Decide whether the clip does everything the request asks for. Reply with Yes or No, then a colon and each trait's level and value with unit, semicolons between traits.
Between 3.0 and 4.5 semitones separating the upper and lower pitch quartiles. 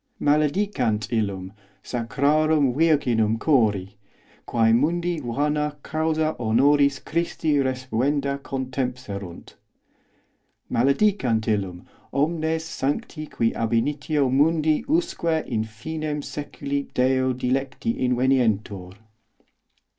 No: average, 4.9 semitones